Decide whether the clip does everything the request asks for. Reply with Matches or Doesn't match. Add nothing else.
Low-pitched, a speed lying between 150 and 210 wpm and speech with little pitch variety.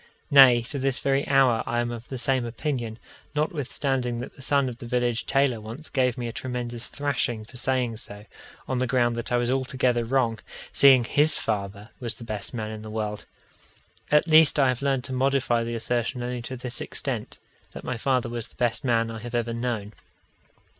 Matches